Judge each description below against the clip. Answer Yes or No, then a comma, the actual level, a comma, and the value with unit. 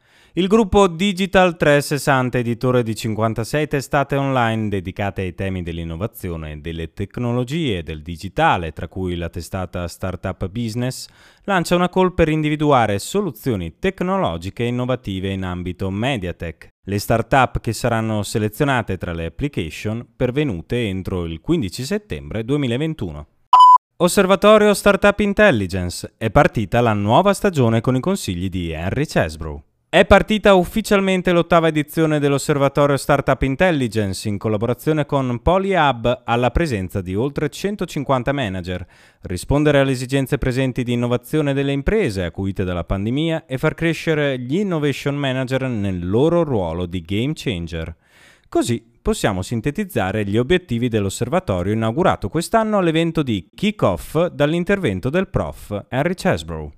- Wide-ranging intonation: Yes, wide, 8.1 semitones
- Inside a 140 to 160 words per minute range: No, average, 130 wpm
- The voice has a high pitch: No, low, 125 Hz